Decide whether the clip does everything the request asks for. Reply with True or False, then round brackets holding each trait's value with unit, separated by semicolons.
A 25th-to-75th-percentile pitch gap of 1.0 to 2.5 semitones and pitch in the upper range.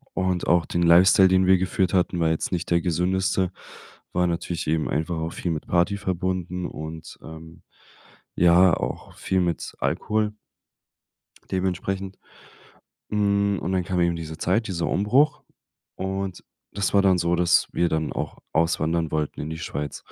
False (2.2 semitones; 90 Hz)